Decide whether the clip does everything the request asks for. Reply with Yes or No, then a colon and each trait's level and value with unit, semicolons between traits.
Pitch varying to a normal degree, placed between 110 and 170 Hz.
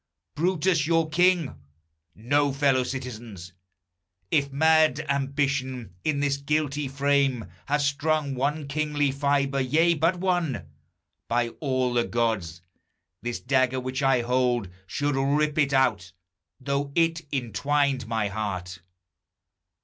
Yes: average, 3.1 semitones; medium, 140 Hz